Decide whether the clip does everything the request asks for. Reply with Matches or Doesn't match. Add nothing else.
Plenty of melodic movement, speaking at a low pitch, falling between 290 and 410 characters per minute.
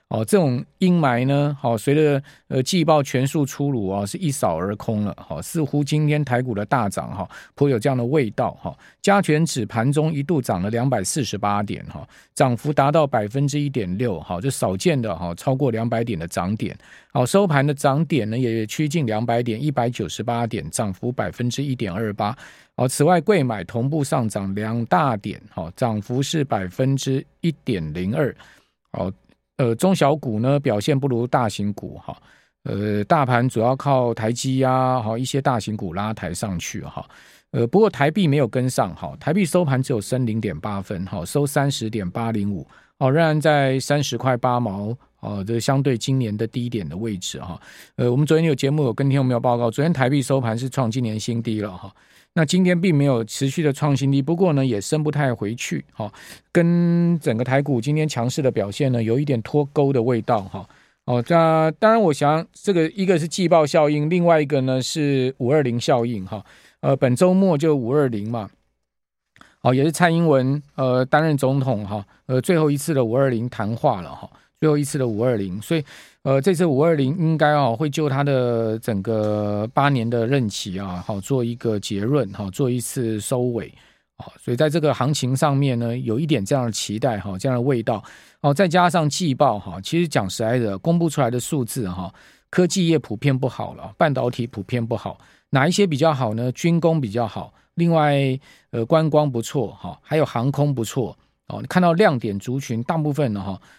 Doesn't match